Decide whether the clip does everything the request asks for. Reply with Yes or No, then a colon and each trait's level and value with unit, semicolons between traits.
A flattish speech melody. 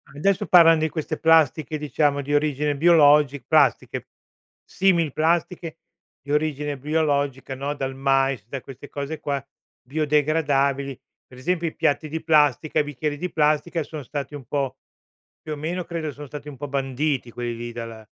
Yes: narrow, 2.3 semitones